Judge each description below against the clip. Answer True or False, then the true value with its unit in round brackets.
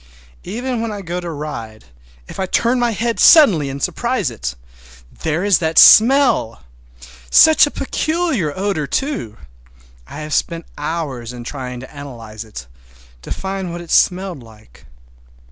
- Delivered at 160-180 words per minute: False (145 wpm)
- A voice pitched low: False (165 Hz)